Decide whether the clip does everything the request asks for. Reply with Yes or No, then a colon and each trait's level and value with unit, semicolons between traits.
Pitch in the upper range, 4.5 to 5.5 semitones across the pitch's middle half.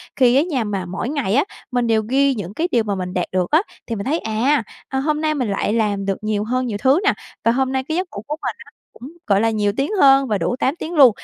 Yes: high, 245 Hz; average, 5.1 semitones